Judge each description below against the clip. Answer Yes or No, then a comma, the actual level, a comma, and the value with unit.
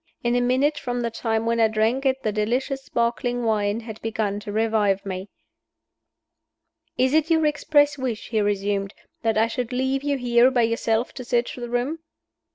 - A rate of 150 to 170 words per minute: No, average, 180 wpm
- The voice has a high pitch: Yes, high, 235 Hz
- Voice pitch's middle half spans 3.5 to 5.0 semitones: No, average, 3.0 semitones